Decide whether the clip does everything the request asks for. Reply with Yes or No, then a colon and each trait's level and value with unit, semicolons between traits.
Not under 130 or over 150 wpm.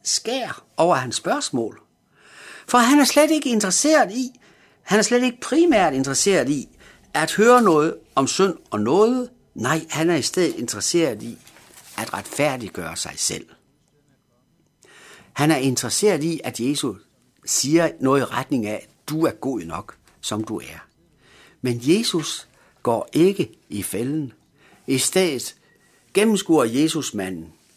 Yes: slow, 145 wpm